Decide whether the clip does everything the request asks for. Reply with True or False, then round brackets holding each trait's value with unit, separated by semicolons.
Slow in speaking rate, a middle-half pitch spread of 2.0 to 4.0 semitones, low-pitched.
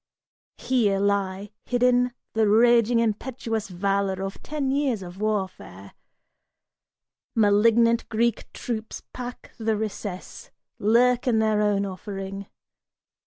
False (105 wpm; 3.1 semitones; 215 Hz)